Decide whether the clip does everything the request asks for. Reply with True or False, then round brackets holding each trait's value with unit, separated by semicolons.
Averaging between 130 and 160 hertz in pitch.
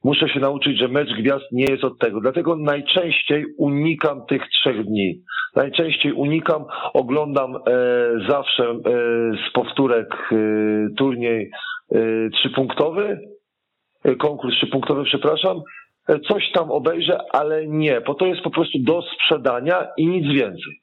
True (140 Hz)